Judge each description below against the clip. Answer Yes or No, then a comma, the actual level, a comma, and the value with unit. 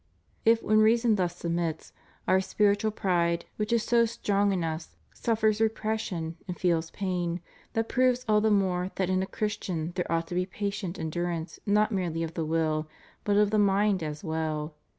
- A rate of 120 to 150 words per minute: No, average, 180 wpm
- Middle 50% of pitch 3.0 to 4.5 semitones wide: Yes, average, 4.1 semitones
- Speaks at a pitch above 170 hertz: Yes, high, 190 Hz